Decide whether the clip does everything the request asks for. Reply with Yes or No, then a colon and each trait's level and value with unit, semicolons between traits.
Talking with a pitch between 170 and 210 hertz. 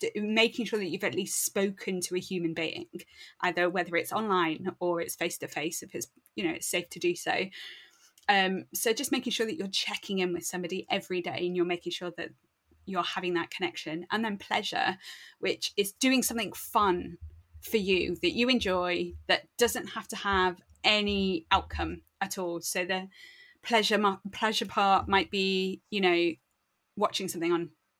Yes: high, 190 Hz